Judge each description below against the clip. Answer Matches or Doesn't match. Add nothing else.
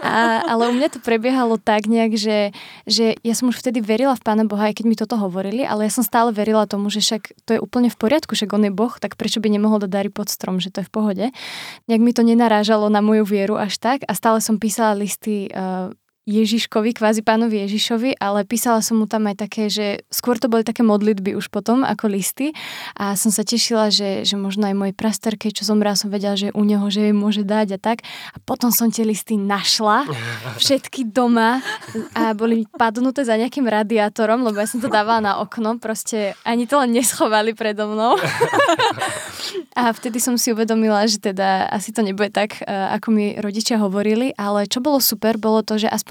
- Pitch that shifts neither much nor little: Doesn't match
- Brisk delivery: Matches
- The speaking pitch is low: Doesn't match